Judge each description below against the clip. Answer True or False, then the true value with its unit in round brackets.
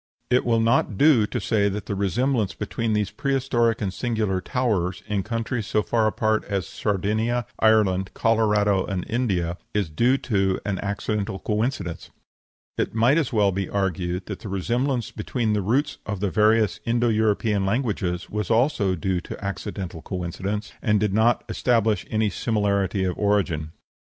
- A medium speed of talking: True (160 wpm)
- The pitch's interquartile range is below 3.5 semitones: True (3.0 semitones)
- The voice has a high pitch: False (105 Hz)